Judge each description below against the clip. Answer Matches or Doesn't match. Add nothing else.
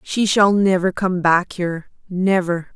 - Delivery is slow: Matches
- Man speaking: Doesn't match